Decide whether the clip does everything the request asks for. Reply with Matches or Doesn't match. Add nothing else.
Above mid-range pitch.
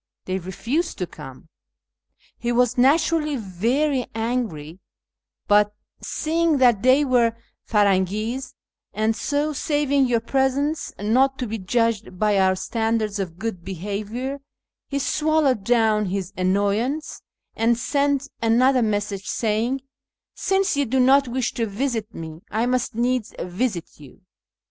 Matches